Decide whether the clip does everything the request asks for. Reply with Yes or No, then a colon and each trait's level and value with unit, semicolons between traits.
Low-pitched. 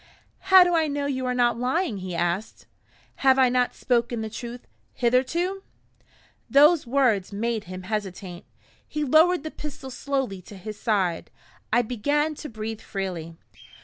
No: high, 245 Hz